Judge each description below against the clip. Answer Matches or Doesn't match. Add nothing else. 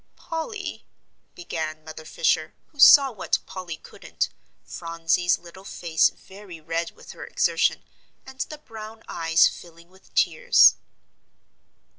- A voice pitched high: Doesn't match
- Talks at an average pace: Doesn't match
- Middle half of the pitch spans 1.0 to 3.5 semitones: Doesn't match